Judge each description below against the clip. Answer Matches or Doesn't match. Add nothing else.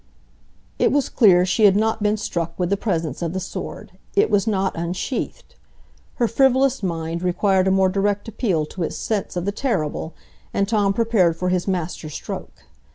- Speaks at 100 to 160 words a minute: Doesn't match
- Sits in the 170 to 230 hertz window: Matches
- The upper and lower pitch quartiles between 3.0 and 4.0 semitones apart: Matches